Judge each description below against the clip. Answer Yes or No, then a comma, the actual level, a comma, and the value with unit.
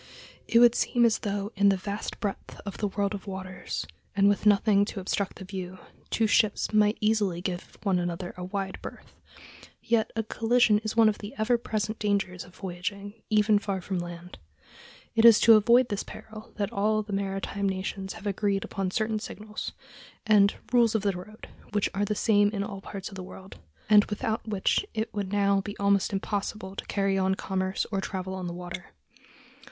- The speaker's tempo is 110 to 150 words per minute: No, average, 195 wpm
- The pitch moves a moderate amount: No, narrow, 1.9 semitones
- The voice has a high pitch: Yes, high, 200 Hz